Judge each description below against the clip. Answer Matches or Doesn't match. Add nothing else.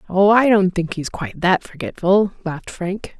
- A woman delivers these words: Matches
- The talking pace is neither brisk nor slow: Matches